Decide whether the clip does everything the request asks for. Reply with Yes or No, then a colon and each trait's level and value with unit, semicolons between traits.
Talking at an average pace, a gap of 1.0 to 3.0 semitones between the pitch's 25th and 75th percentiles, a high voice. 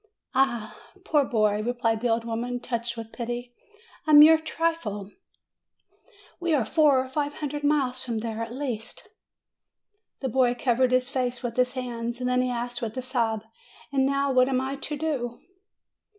Yes: average, 165 wpm; average, 2.7 semitones; very high, 250 Hz